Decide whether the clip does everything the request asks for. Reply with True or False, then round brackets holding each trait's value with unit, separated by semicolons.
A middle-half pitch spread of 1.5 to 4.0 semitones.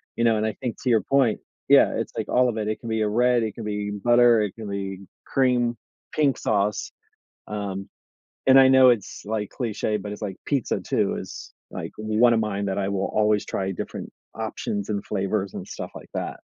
True (2.9 semitones)